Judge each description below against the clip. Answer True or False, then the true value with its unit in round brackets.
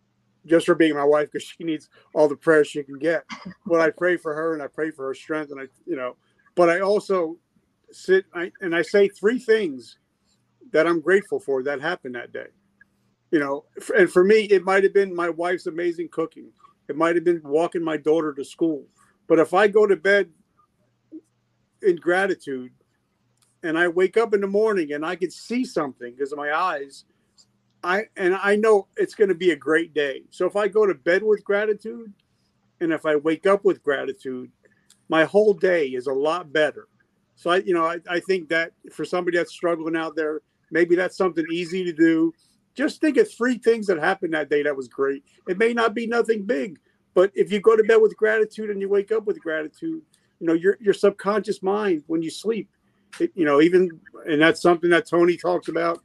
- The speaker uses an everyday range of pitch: False (6.2 semitones)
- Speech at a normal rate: False (210 wpm)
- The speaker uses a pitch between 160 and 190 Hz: True (185 Hz)